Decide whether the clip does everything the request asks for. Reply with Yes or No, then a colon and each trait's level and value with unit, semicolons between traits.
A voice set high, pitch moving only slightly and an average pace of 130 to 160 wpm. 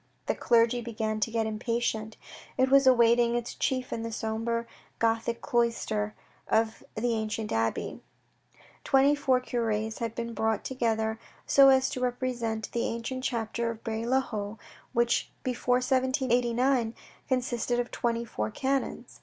Yes: high, 235 Hz; narrow, 2.1 semitones; average, 145 wpm